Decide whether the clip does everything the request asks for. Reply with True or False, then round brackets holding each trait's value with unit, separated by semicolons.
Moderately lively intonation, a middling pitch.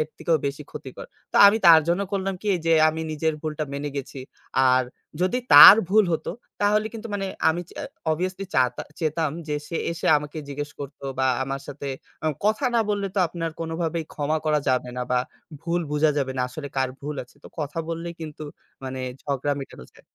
True (3.4 semitones; 155 Hz)